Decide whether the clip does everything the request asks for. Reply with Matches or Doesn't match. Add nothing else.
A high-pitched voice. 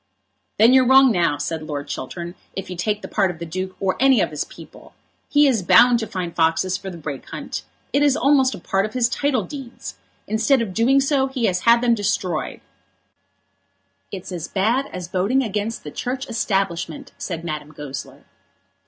Matches